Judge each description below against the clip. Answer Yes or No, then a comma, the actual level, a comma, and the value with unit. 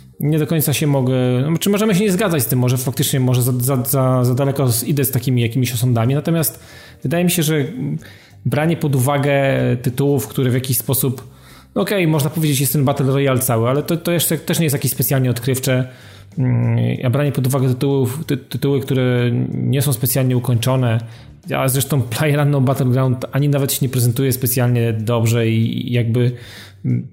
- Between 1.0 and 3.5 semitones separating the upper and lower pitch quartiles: Yes, narrow, 2.5 semitones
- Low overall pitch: Yes, low, 130 Hz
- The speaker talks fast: Yes, fast, 190 wpm